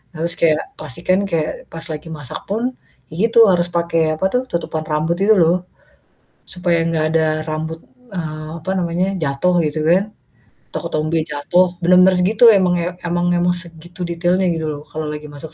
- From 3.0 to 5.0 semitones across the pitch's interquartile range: No, narrow, 2.4 semitones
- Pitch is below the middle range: No, medium, 170 Hz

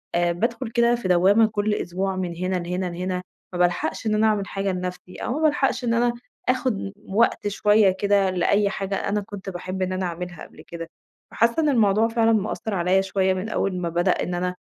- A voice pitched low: No, high, 195 Hz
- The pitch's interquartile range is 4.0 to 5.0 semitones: No, average, 3.2 semitones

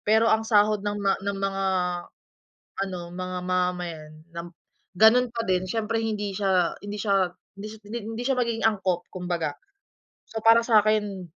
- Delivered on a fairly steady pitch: No, average, 3.3 semitones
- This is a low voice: No, high, 200 Hz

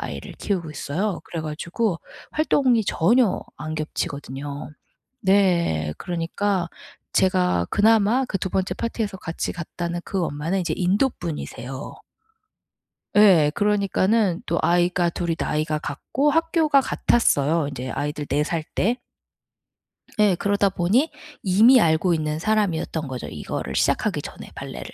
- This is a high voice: No, medium, 180 Hz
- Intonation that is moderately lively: Yes, average, 5.0 semitones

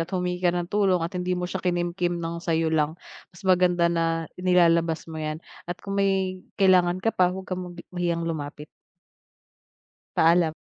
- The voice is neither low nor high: Yes, medium, 175 Hz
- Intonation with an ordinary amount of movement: No, narrow, 1.7 semitones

